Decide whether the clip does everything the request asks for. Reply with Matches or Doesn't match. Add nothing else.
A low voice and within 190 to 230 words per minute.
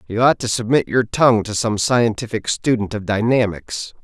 Doesn't match